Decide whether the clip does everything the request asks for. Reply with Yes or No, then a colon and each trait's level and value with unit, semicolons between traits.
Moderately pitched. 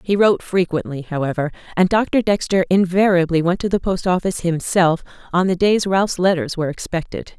Yes: medium, 180 Hz